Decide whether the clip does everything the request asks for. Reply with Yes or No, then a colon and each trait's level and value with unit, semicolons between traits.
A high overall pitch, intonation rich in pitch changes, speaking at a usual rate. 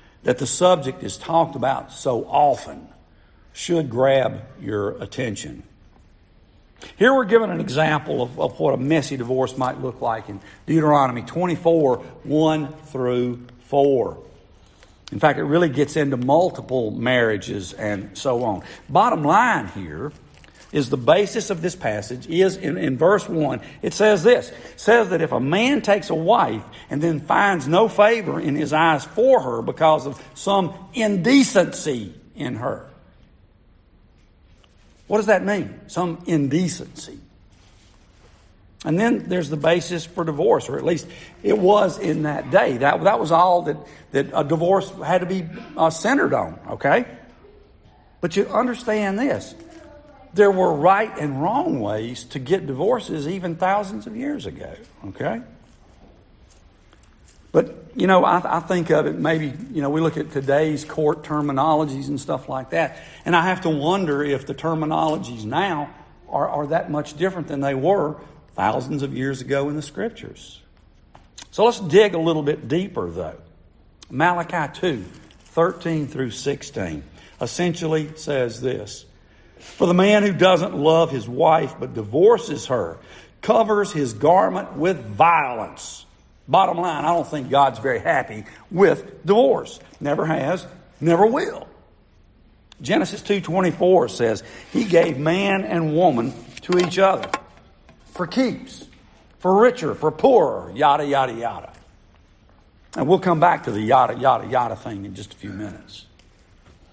No: medium, 155 Hz; wide, 6.2 semitones; average, 150 wpm